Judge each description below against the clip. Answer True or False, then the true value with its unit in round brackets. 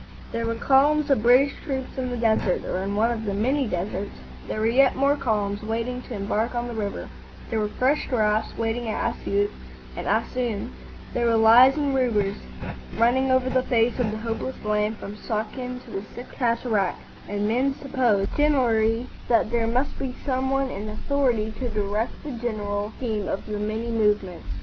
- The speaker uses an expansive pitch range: False (3.3 semitones)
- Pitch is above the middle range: True (230 Hz)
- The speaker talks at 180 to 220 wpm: True (185 wpm)